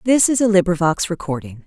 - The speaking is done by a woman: Yes, female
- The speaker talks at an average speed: Yes, average, 180 wpm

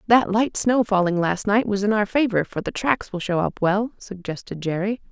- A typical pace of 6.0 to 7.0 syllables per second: No, 5.0 syllables/s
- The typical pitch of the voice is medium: No, high, 205 Hz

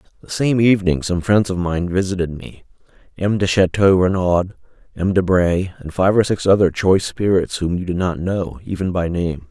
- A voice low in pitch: Yes, very low, 90 Hz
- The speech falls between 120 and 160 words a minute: No, average, 185 wpm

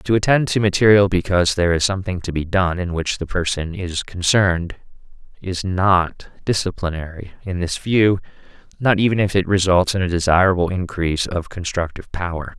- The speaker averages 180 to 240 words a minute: No, average, 165 wpm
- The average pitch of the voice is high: No, very low, 90 Hz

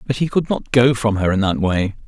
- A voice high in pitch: No, low, 115 Hz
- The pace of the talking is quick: Yes, fast, 290 wpm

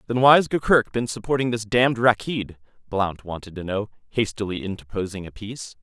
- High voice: No, low, 110 Hz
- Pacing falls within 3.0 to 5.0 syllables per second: No, 5.5 syllables/s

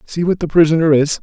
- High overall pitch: No, medium, 160 Hz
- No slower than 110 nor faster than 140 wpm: No, fast, 245 wpm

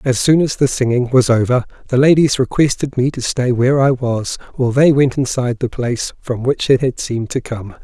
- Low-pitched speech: Yes, low, 130 Hz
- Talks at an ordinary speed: No, fast, 220 wpm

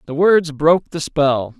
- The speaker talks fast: No, average, 190 wpm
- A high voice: No, medium, 150 Hz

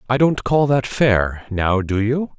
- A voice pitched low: Yes, low, 120 Hz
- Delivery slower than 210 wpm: Yes, average, 200 wpm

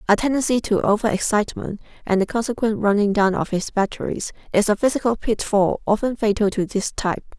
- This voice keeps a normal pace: Yes, average, 180 wpm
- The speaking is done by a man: No, female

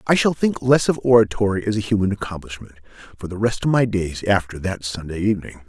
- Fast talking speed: Yes, fast, 210 wpm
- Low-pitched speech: Yes, low, 105 Hz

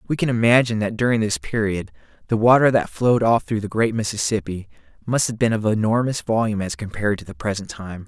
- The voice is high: No, low, 110 Hz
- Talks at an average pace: No, fast, 210 wpm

